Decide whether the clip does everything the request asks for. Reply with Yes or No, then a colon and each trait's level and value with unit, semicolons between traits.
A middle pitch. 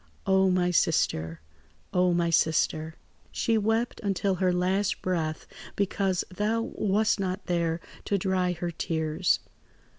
Yes: medium, 180 Hz